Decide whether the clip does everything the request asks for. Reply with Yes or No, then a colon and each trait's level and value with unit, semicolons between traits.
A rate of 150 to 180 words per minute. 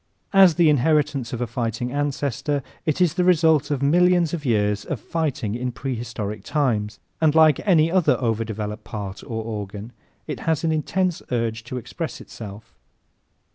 Yes: average, 165 wpm